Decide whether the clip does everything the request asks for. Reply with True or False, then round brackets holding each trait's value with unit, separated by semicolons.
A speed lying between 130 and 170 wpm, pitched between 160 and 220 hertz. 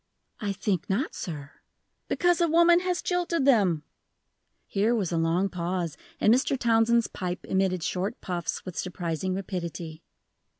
True (140 wpm; 190 Hz)